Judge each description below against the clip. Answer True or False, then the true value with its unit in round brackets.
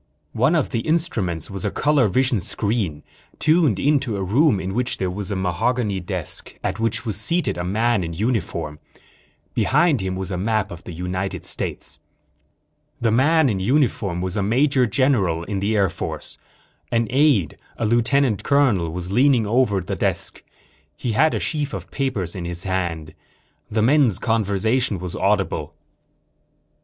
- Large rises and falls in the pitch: True (5.8 semitones)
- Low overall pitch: True (105 Hz)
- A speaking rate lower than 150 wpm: False (165 wpm)